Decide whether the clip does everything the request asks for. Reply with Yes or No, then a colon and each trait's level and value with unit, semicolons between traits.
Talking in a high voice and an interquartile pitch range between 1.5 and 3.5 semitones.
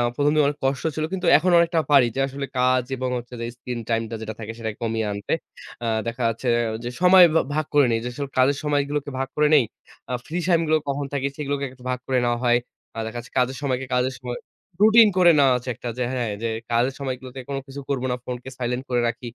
No: low, 130 Hz; average, 2.8 semitones